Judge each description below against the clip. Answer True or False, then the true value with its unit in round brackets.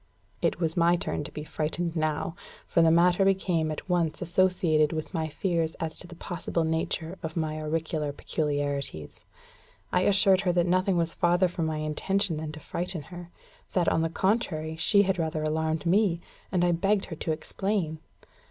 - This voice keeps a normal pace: True (180 wpm)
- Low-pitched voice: False (165 Hz)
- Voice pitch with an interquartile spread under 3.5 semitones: True (2.4 semitones)